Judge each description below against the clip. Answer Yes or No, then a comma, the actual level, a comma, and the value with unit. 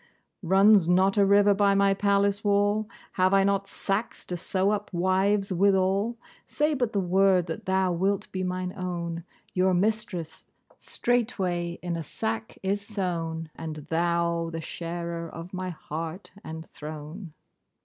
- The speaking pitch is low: No, medium, 185 Hz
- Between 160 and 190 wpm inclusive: No, average, 150 wpm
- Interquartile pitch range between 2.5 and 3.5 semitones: Yes, average, 2.9 semitones